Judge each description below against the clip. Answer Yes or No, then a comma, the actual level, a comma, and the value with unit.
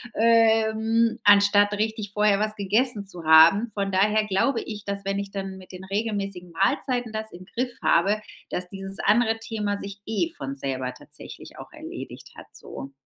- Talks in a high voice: Yes, high, 205 Hz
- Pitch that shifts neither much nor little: No, narrow, 2.3 semitones